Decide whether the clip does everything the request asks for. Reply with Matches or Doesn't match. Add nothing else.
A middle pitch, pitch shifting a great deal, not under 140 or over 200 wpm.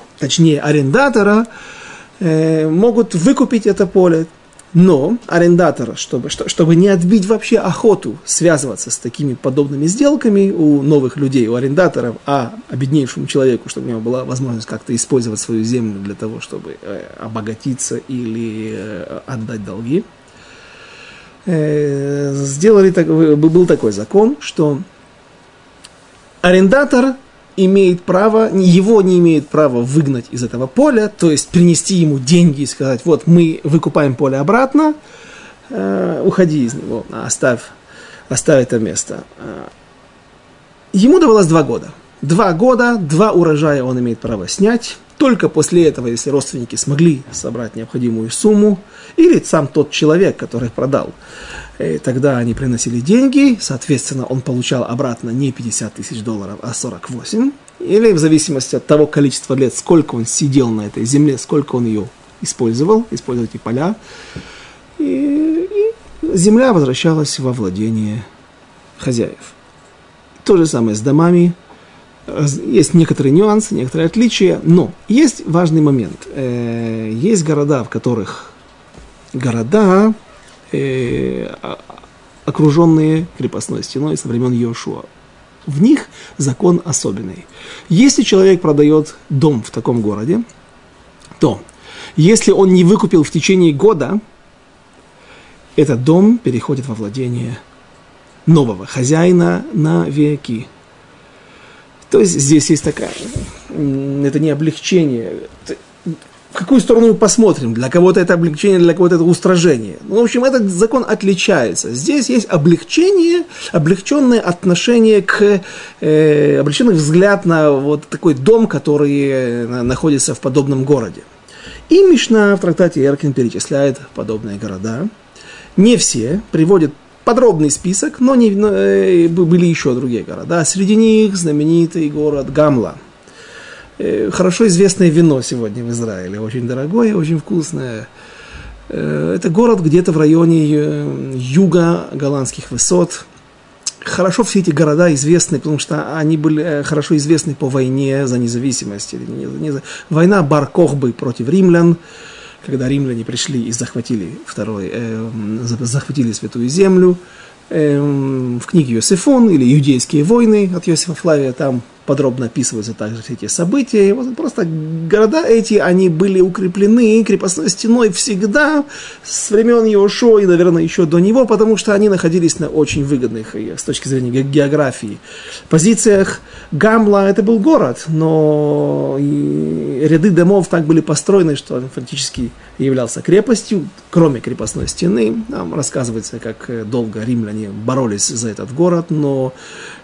Doesn't match